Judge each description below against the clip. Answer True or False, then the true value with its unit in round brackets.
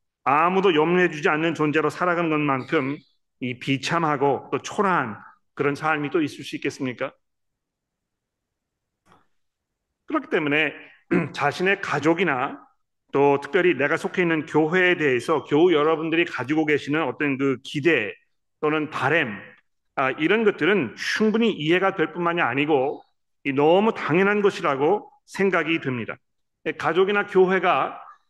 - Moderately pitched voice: True (160 Hz)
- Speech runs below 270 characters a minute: False (285 characters per minute)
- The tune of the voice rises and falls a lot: False (4.4 semitones)